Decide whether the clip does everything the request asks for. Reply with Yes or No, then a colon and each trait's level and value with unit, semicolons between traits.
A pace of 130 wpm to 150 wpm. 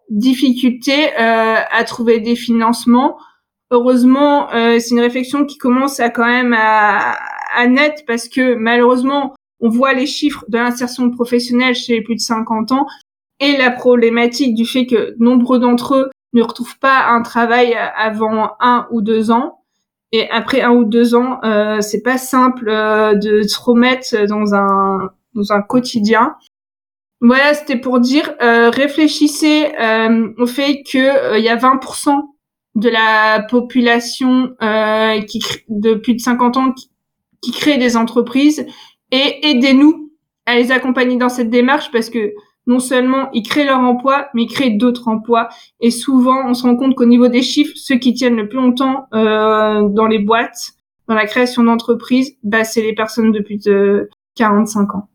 No: average, 175 wpm